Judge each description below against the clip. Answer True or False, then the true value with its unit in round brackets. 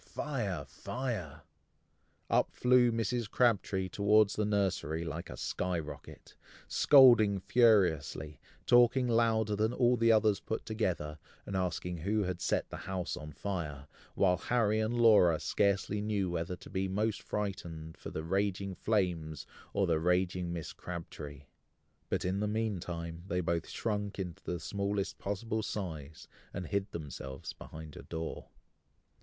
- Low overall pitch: True (95 Hz)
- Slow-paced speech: False (145 wpm)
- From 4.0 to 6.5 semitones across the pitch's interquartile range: True (4.3 semitones)